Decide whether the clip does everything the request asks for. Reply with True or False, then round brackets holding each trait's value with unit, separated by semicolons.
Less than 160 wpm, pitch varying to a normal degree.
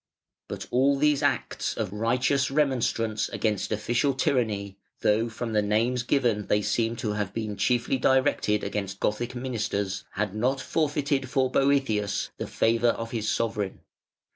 True (145 wpm; 3.9 semitones)